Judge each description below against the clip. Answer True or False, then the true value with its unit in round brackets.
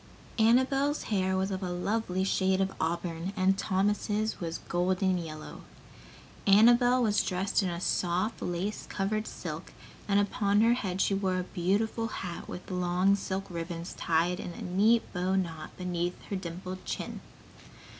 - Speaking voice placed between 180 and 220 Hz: True (190 Hz)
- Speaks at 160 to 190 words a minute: False (150 wpm)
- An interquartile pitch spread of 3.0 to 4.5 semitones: False (2.5 semitones)